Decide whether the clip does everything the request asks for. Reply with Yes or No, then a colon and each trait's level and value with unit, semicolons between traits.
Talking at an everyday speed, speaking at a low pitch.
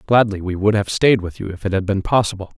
No: fast, 280 wpm; low, 100 Hz